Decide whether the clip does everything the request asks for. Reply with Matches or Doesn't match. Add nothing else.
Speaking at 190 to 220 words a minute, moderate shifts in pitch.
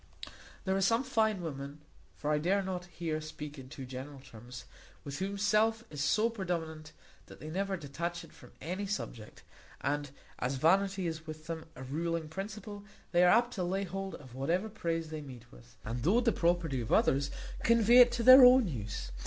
Doesn't match